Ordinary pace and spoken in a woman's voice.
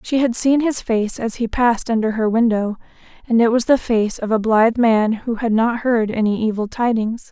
No: fast, 220 wpm; female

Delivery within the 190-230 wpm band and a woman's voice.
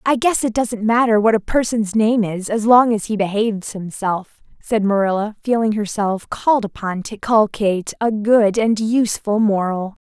No: average, 175 wpm; female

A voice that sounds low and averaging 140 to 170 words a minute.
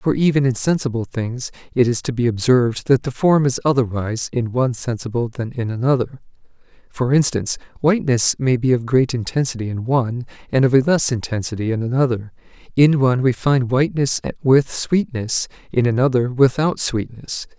Yes: low, 125 Hz; average, 165 wpm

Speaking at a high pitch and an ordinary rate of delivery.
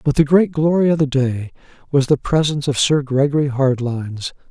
No: medium, 140 Hz; average, 185 wpm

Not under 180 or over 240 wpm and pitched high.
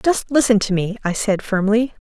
Yes: average, 200 wpm; high, 220 Hz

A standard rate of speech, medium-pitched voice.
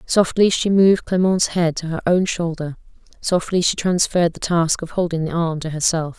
Yes: average, 195 wpm; medium, 170 Hz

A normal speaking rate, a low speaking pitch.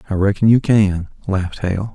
Yes: average, 185 wpm; low, 100 Hz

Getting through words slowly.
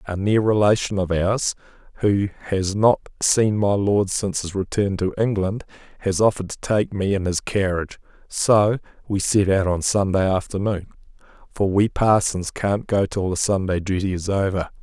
No: average, 170 wpm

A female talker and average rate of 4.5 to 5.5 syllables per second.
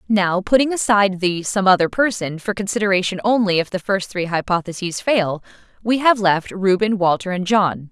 Yes: female; 5.2 syllables/s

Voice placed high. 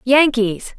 Yes: very high, 250 Hz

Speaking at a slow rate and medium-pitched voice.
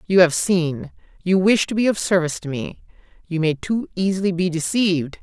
No: average, 185 wpm; medium, 180 Hz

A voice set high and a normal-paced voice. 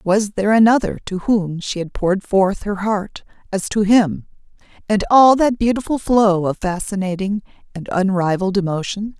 Yes: high, 200 Hz; average, 155 wpm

